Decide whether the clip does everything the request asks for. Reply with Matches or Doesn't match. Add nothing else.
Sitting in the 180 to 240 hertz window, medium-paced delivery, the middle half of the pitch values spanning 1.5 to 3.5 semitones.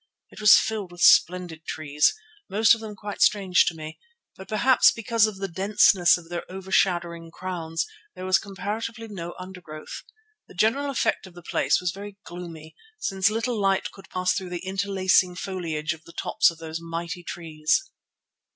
Matches